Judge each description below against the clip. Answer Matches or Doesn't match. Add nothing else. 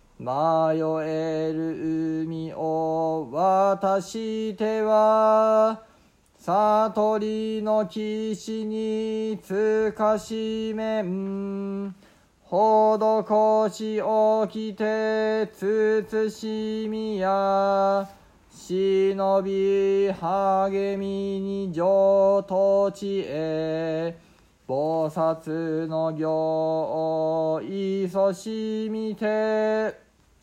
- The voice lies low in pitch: Doesn't match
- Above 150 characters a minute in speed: Doesn't match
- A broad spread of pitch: Doesn't match